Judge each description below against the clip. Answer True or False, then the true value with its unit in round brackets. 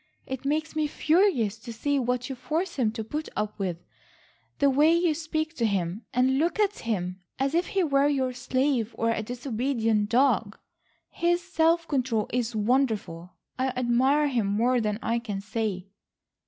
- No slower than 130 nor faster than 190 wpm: True (170 wpm)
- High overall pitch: True (250 Hz)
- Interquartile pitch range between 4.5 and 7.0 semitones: True (5.1 semitones)